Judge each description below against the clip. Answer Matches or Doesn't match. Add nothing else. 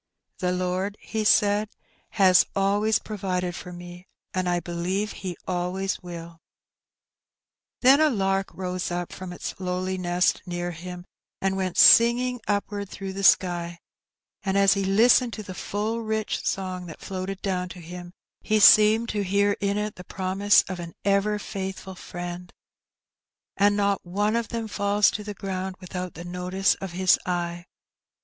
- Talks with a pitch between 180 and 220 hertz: Matches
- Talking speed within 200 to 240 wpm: Doesn't match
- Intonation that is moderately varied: Doesn't match